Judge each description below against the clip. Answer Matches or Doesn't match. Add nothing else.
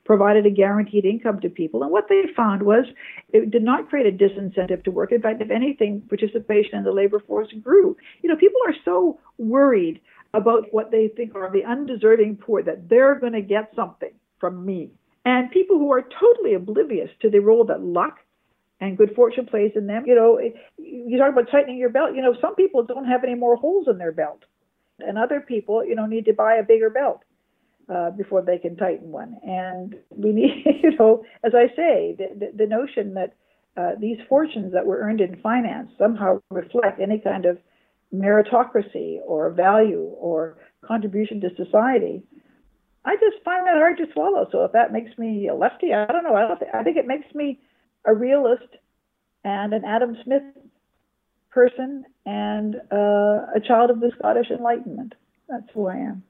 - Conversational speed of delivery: Matches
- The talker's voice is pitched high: Matches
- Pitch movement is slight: Doesn't match